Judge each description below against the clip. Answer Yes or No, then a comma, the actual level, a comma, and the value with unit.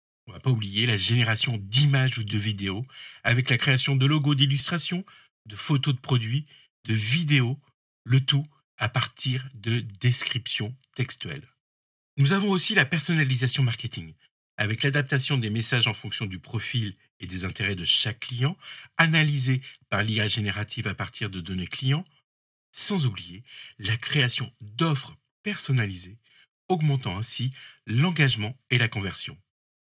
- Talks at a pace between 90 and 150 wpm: Yes, slow, 145 wpm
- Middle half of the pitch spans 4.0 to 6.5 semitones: Yes, average, 4.3 semitones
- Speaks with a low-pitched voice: Yes, low, 125 Hz